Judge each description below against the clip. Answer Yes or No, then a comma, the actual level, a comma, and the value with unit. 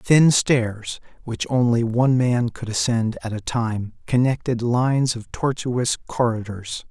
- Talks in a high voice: No, low, 120 Hz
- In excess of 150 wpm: No, average, 140 wpm